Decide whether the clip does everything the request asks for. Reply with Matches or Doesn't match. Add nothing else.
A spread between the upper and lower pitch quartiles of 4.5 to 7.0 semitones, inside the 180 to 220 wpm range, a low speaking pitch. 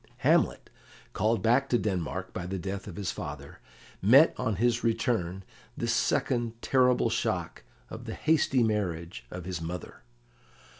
Doesn't match